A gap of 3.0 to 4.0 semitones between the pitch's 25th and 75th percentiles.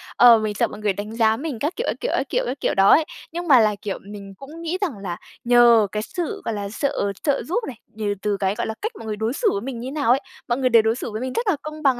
No: wide, 5.6 semitones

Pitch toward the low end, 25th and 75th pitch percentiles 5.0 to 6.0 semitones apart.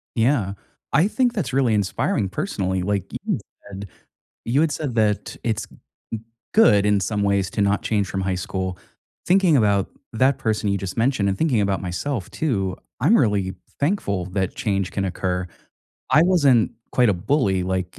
Yes: low, 105 Hz; wide, 5.4 semitones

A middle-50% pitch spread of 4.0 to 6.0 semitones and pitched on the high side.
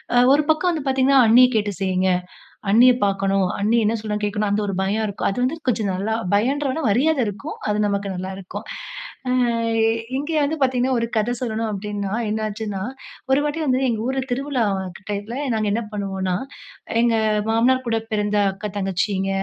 Yes: average, 4.3 semitones; high, 220 Hz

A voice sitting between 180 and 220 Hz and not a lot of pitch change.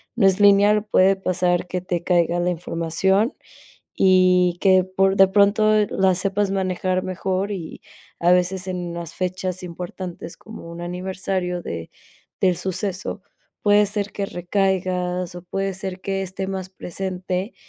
Yes: medium, 185 Hz; narrow, 1.5 semitones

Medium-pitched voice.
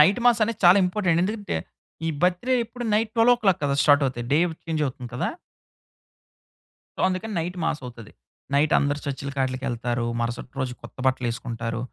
Yes: medium, 150 Hz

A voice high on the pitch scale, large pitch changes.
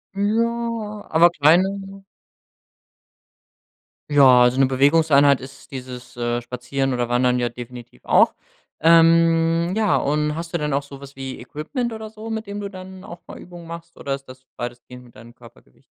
No: medium, 150 Hz; wide, 6.5 semitones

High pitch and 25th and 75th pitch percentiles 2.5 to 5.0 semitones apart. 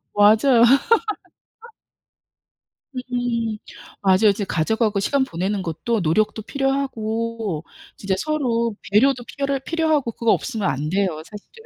Yes: high, 225 Hz; average, 4.5 semitones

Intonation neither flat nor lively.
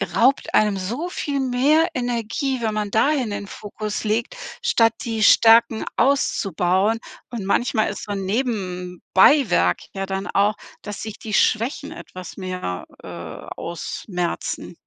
Yes: average, 4.2 semitones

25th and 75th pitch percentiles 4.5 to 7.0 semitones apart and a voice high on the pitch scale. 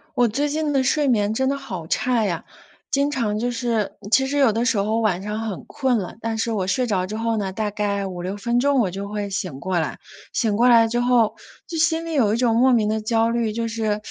No: average, 3.2 semitones; high, 225 Hz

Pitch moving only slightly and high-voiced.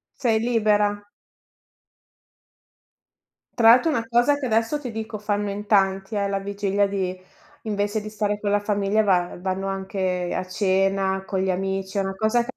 Yes: narrow, 2.1 semitones; high, 205 Hz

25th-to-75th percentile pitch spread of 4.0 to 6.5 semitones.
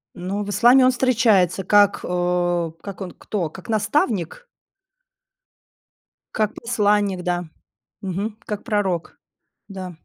No: average, 3.2 semitones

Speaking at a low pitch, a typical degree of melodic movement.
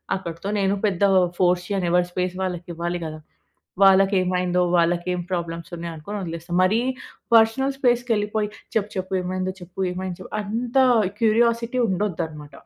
No: medium, 185 Hz; average, 3.2 semitones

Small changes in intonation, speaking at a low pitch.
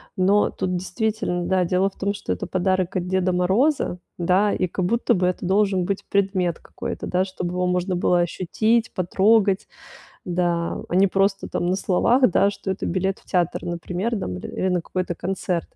No: narrow, 1.8 semitones; medium, 185 Hz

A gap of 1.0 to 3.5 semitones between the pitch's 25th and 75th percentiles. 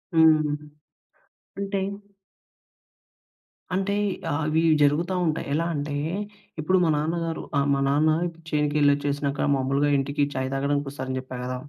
Yes: narrow, 2.4 semitones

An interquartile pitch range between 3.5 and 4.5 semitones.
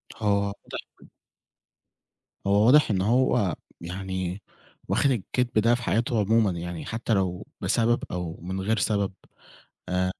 Yes: average, 3.8 semitones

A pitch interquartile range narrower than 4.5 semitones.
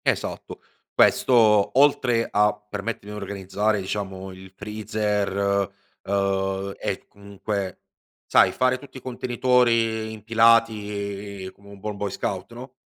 Yes: narrow, 2.5 semitones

